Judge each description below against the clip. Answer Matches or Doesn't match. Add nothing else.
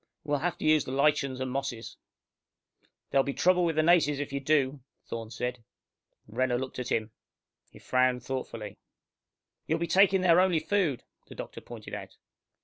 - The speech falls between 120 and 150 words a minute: Doesn't match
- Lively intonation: Doesn't match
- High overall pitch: Doesn't match